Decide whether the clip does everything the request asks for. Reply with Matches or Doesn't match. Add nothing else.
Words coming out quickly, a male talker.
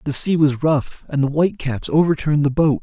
Matches